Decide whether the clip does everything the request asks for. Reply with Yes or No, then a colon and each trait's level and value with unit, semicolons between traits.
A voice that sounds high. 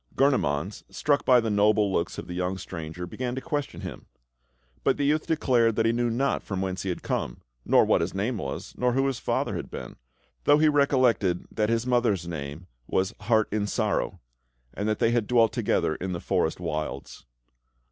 No: low, 110 Hz